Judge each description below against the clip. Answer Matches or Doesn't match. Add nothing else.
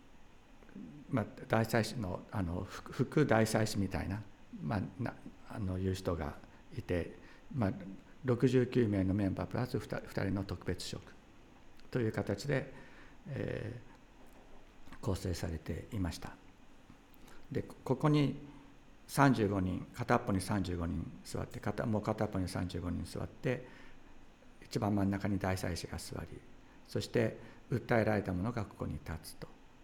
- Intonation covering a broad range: Doesn't match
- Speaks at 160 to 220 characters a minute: Matches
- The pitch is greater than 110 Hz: Doesn't match